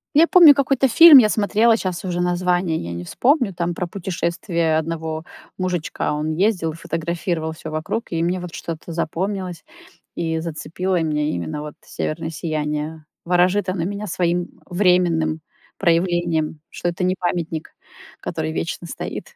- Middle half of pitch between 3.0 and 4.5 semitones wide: No, narrow, 2.6 semitones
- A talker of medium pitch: Yes, medium, 170 Hz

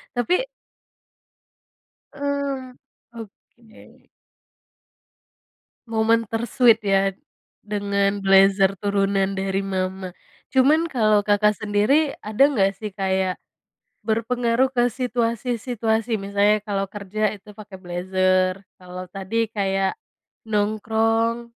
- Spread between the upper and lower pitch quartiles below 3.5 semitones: Yes, average, 3.0 semitones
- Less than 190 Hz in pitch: No, high, 210 Hz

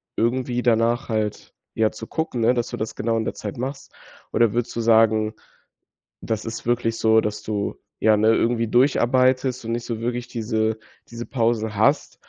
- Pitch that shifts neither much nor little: No, narrow, 1.6 semitones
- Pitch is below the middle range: Yes, low, 115 Hz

